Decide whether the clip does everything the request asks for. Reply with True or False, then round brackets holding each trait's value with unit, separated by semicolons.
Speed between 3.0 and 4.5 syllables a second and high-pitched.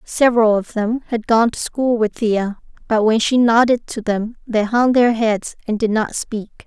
True (4.3 syllables/s; 225 Hz)